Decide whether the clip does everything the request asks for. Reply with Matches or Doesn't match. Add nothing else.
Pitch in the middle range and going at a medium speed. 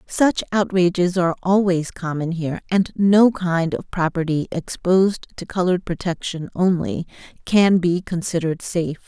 Doesn't match